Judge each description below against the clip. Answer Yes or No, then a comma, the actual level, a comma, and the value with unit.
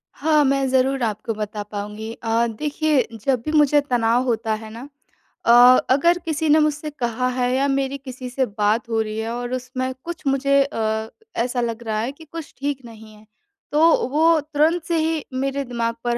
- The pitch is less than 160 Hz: No, very high, 255 Hz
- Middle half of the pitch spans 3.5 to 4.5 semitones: Yes, average, 4.1 semitones